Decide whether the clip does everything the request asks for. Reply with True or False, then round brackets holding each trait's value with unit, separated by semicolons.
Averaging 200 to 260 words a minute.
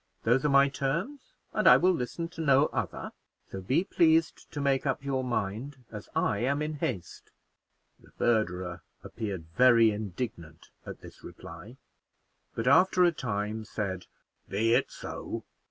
False (155 wpm)